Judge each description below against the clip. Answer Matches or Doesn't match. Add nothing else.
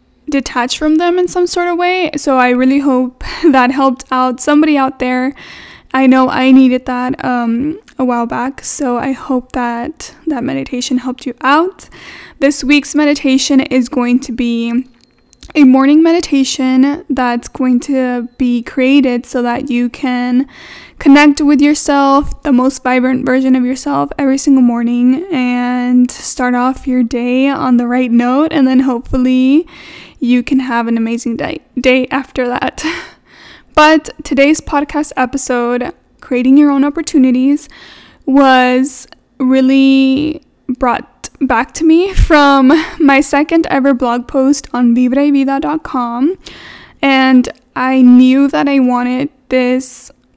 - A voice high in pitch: Matches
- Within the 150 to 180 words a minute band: Doesn't match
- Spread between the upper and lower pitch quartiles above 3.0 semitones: Doesn't match